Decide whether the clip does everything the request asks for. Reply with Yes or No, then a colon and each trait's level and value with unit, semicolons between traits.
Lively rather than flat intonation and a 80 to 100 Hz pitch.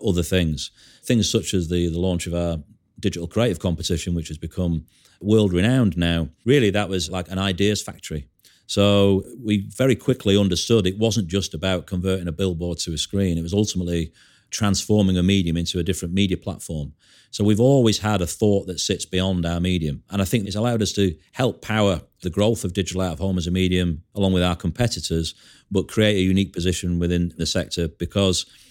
No: average, 3.1 semitones; very low, 95 Hz